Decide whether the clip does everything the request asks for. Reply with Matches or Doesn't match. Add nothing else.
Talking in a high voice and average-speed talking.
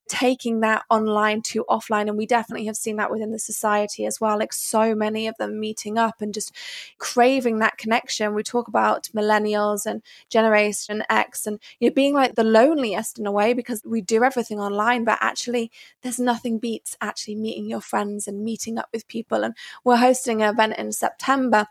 Matches